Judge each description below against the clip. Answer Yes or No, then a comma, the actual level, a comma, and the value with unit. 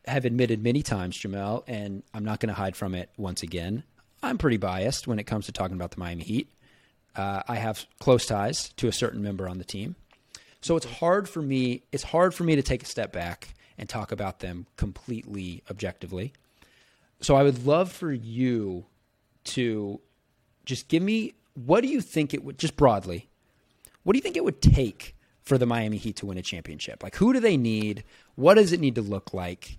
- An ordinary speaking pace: No, fast, 210 wpm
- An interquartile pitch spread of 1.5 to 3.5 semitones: No, wide, 5.6 semitones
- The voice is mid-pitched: No, low, 110 Hz